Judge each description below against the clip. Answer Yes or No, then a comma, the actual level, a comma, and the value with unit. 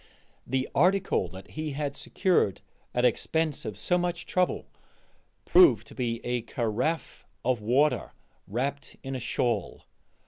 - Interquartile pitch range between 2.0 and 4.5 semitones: No, average, 5.3 semitones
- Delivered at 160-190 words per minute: No, slow, 135 wpm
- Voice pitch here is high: No, low, 135 Hz